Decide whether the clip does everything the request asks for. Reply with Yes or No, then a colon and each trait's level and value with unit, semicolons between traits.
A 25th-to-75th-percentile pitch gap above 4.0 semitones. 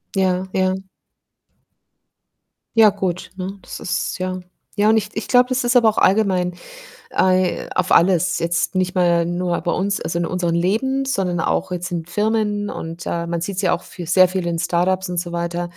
No: narrow, 2.6 semitones